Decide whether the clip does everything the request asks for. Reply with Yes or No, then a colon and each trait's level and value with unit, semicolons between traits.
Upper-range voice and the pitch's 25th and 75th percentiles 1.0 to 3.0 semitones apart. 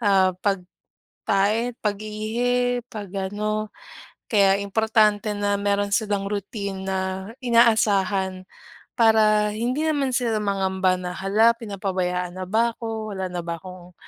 Yes: high, 205 Hz; narrow, 2.6 semitones